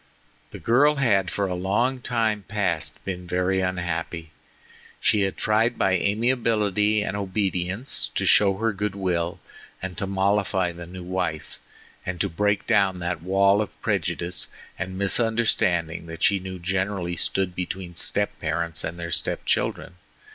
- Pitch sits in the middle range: No, very low, 95 Hz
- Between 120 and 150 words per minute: Yes, average, 145 wpm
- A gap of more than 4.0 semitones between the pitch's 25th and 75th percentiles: No, average, 2.7 semitones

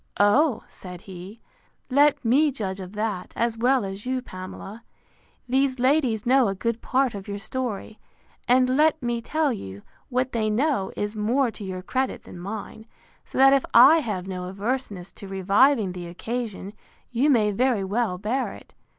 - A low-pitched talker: No, high, 225 Hz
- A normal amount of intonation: Yes, average, 4.8 semitones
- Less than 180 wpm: Yes, average, 170 wpm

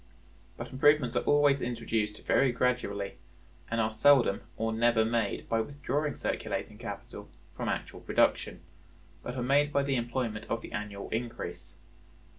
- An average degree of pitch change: Yes, average, 3.6 semitones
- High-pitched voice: No, low, 120 Hz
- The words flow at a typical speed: Yes, average, 145 wpm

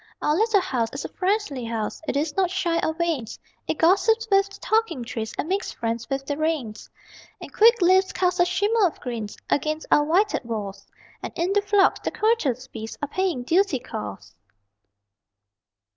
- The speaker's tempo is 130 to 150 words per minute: No, average, 180 wpm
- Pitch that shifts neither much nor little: No, wide, 7.6 semitones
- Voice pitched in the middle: No, very high, 330 Hz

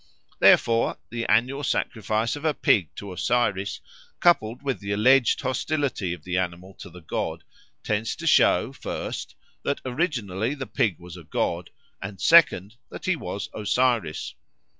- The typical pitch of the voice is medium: No, low, 110 Hz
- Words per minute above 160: No, average, 150 wpm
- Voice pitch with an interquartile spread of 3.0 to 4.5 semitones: No, wide, 5.5 semitones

